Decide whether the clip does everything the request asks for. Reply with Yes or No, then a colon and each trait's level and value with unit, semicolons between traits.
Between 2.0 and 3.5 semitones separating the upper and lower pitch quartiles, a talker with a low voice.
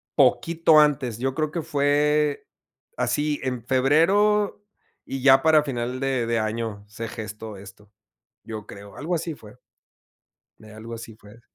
No: average, 5.1 semitones; low, 130 Hz